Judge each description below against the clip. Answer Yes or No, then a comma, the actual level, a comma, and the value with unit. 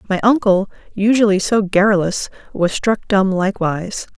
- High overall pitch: Yes, high, 200 Hz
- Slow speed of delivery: Yes, slow, 130 wpm